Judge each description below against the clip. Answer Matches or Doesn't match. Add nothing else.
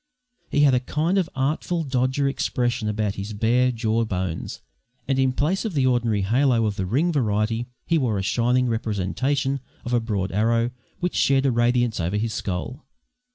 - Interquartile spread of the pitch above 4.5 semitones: Doesn't match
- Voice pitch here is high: Doesn't match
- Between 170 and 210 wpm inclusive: Matches